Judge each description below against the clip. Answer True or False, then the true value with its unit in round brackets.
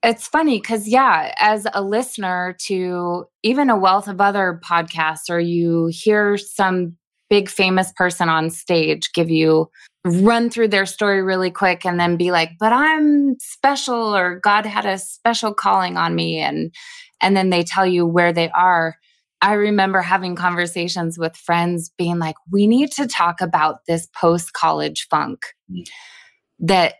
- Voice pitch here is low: False (185 Hz)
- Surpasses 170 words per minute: False (160 wpm)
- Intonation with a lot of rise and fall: False (3.4 semitones)